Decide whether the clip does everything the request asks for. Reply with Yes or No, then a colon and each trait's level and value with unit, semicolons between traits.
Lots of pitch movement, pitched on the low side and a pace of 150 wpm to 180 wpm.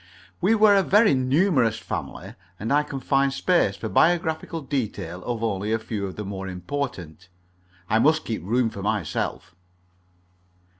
Yes: wide, 6.9 semitones; low, 120 Hz; average, 155 wpm